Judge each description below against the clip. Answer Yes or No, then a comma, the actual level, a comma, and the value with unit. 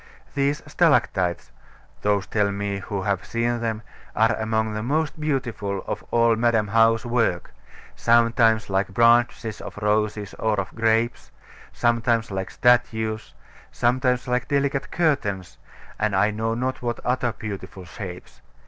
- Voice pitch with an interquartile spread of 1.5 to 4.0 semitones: Yes, average, 2.9 semitones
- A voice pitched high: No, low, 115 Hz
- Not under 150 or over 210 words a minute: No, slow, 135 wpm